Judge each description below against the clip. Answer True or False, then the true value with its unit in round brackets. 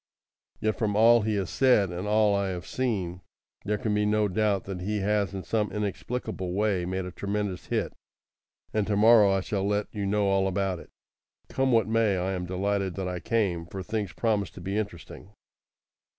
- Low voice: True (100 Hz)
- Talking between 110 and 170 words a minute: False (195 wpm)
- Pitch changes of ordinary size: False (2.2 semitones)